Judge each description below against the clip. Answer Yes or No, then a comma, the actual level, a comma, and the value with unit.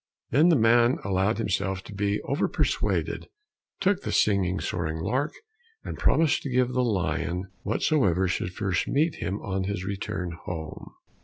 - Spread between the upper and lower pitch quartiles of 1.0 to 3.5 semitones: No, average, 5.3 semitones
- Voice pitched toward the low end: Yes, low, 100 Hz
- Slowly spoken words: No, average, 155 wpm